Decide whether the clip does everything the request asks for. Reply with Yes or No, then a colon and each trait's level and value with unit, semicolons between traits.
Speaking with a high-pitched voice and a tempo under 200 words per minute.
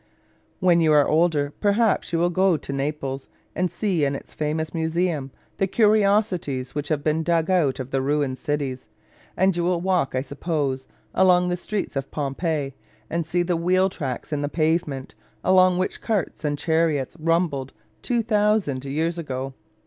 No: medium, 160 Hz; average, 165 wpm